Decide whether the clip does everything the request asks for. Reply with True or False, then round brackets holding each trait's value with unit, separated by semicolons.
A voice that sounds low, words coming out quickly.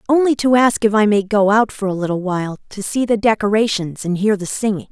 False (210 Hz; 245 wpm)